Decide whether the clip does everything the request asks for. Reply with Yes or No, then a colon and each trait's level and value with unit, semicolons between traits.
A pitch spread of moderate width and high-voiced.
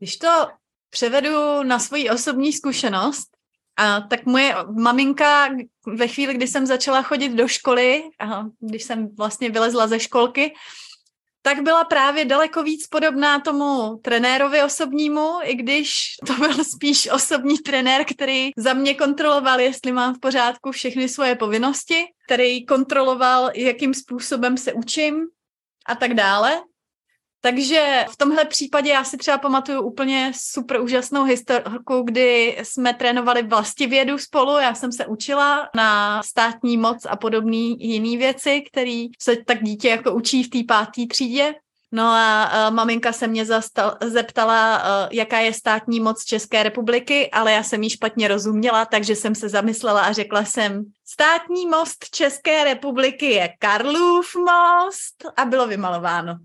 Yes: average, 3.9 semitones; very high, 255 Hz